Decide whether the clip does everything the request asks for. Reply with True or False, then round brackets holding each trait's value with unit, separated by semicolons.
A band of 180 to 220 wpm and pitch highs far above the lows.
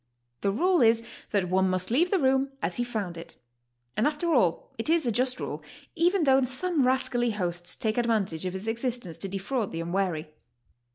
True (190 wpm; 6.0 semitones)